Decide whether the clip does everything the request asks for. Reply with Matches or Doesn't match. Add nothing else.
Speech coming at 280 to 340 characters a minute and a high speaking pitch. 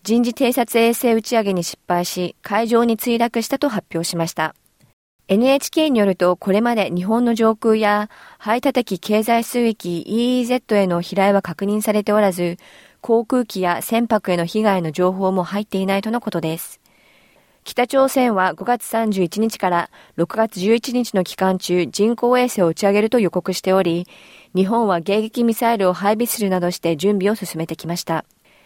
Matches